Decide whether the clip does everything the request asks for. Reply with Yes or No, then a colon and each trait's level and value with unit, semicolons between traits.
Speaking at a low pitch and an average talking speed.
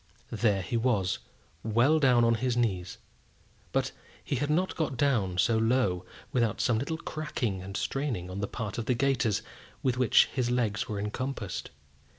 Yes: low, 115 Hz; average, 165 wpm